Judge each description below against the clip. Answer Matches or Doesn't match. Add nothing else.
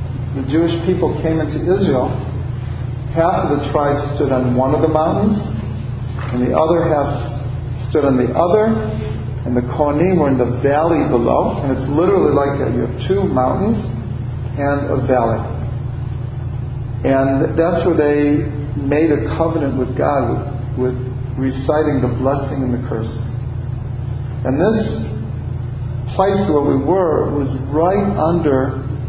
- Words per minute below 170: Matches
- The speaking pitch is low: Matches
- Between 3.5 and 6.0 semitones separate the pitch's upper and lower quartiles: Doesn't match